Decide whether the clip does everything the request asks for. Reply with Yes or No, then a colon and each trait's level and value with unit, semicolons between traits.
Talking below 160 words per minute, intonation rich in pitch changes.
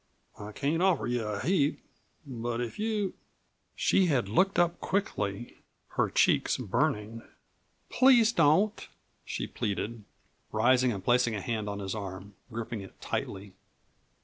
Yes: average, 140 wpm; wide, 8.3 semitones